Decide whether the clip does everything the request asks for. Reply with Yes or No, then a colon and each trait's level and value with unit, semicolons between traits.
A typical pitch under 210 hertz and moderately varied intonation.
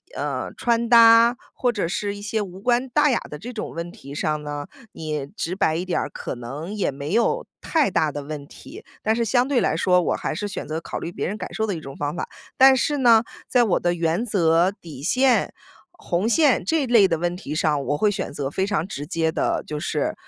No: high, 190 Hz; wide, 7.0 semitones